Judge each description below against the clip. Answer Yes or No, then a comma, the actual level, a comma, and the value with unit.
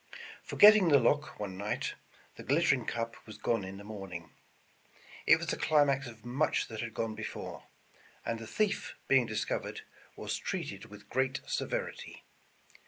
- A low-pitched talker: Yes, low, 115 Hz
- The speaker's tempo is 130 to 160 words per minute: Yes, average, 155 wpm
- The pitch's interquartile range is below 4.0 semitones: No, average, 4.7 semitones